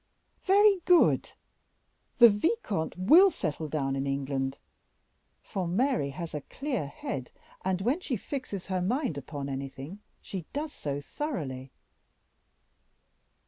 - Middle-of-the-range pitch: Yes, medium, 180 Hz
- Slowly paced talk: Yes, slow, 120 wpm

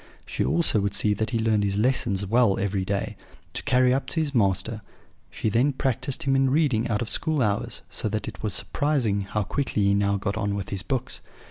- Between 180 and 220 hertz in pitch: No, low, 110 Hz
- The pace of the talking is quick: Yes, fast, 220 wpm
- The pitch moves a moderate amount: Yes, average, 4.5 semitones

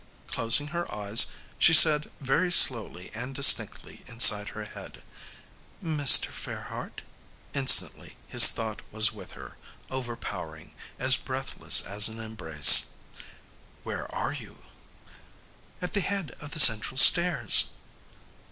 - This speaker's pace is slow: Yes, slow, 115 wpm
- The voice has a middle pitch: No, low, 120 Hz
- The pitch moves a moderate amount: No, wide, 5.8 semitones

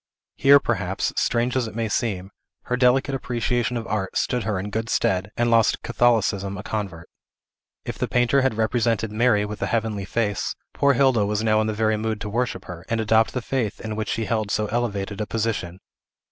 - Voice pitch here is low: Yes, low, 110 Hz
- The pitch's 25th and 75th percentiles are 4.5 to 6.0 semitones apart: No, narrow, 2.6 semitones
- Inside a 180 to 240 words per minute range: Yes, average, 200 wpm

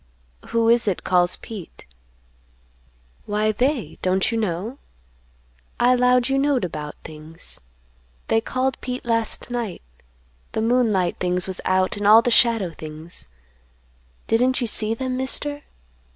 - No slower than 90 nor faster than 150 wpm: Yes, slow, 135 wpm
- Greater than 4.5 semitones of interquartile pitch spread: Yes, average, 5.1 semitones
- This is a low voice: No, high, 225 Hz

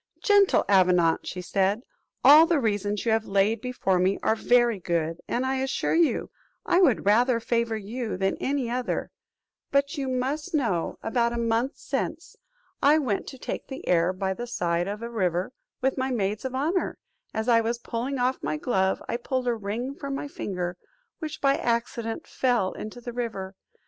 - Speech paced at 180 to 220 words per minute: Yes, average, 185 wpm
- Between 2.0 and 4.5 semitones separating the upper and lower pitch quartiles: No, average, 4.9 semitones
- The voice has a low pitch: No, high, 235 Hz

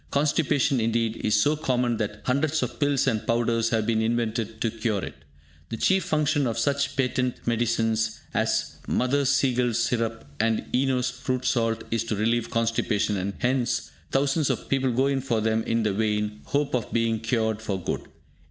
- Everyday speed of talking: Yes, average, 175 wpm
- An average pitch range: Yes, average, 3.0 semitones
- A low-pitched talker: Yes, low, 115 Hz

